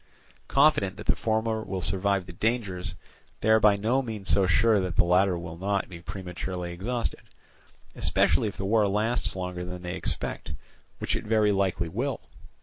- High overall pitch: No, low, 100 Hz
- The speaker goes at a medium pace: Yes, average, 175 wpm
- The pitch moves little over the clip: No, average, 3.4 semitones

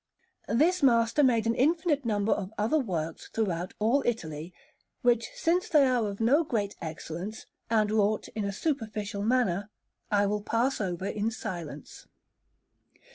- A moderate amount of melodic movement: Yes, average, 3.9 semitones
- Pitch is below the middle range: No, high, 220 Hz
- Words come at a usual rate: Yes, average, 145 wpm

